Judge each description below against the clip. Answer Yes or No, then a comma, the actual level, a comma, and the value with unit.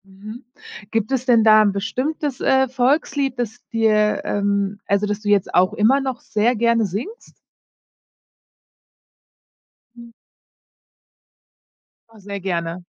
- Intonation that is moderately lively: Yes, average, 3.6 semitones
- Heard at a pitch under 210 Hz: No, high, 220 Hz